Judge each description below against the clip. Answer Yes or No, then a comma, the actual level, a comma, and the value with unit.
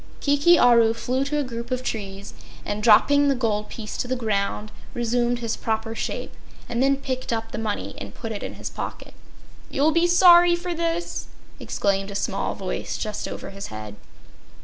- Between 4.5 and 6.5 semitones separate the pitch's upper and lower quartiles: Yes, average, 4.8 semitones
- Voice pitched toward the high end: Yes, high, 235 Hz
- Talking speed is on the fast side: No, average, 185 wpm